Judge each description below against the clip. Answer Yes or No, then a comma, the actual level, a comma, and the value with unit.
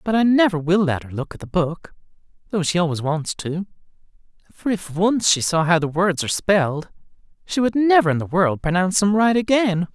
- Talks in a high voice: No, medium, 180 Hz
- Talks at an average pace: No, fast, 210 wpm